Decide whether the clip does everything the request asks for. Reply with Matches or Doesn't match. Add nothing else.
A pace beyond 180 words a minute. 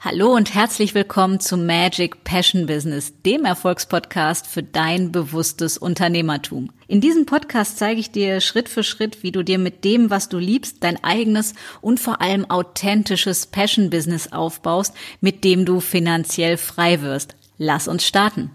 Doesn't match